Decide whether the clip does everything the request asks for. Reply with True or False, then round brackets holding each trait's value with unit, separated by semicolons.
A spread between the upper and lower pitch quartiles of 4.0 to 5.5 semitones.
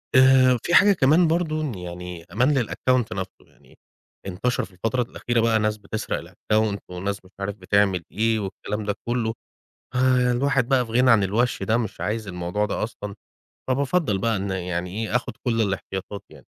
True (4.3 semitones)